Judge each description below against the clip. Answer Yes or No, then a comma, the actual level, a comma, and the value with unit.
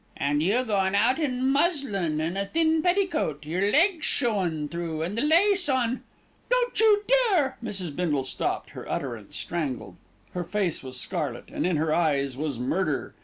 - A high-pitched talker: Yes, high, 195 Hz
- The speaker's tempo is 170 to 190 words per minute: Yes, average, 180 wpm